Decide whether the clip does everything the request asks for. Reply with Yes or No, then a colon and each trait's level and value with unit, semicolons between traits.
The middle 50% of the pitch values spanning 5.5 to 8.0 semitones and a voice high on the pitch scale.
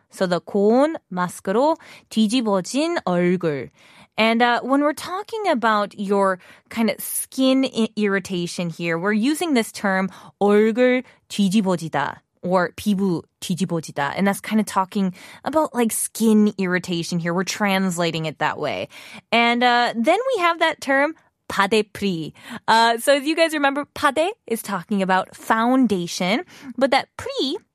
Yes: wide, 5.9 semitones; high, 215 Hz